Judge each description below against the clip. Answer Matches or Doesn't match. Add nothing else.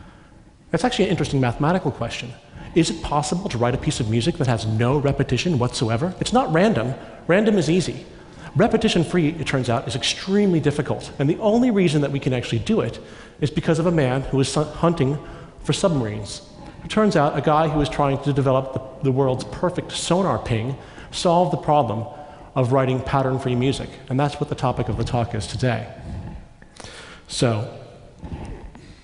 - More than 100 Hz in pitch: Matches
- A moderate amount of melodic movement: Matches